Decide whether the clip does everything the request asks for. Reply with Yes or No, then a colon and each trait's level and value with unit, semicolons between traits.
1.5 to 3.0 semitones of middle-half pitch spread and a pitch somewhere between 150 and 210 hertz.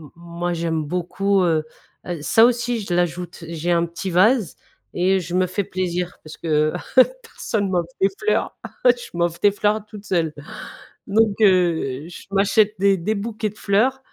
No: average, 3.4 semitones; medium, 185 Hz